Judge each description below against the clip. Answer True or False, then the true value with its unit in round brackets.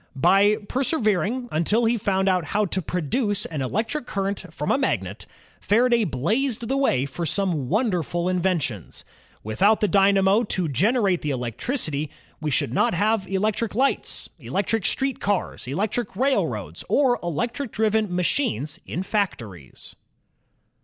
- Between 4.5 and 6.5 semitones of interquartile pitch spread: True (5.2 semitones)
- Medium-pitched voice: False (195 Hz)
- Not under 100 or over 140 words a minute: True (135 wpm)